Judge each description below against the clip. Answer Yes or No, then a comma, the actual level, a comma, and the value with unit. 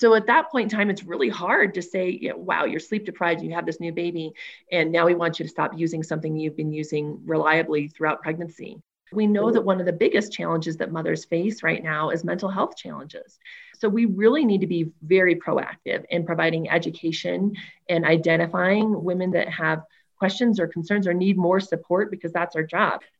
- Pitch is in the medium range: Yes, medium, 170 Hz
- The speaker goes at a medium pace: No, fast, 210 wpm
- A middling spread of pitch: Yes, average, 3.4 semitones